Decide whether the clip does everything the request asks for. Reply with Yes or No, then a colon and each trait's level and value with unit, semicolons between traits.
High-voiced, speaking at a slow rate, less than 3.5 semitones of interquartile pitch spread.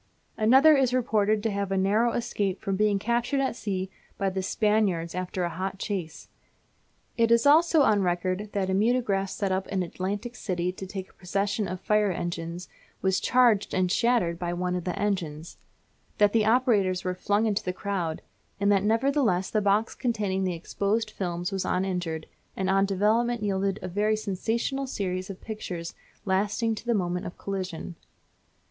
No: high, 195 Hz; average, 180 wpm; average, 2.9 semitones